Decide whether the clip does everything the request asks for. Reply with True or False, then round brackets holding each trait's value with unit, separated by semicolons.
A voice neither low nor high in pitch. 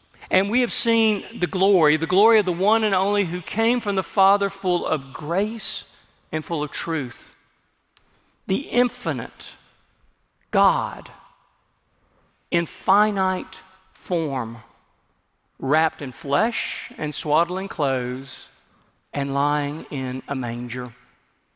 True (165 Hz)